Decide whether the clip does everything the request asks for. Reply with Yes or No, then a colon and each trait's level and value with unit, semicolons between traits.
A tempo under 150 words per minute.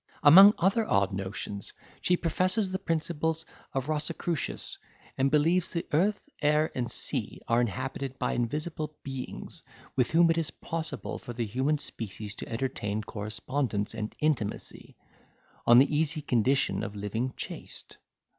Yes: average, 140 wpm